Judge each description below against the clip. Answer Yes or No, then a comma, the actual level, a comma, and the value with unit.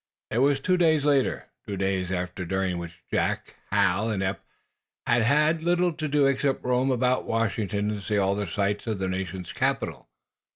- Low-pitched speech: Yes, low, 110 Hz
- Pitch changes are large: Yes, wide, 6.2 semitones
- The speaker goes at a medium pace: Yes, average, 175 wpm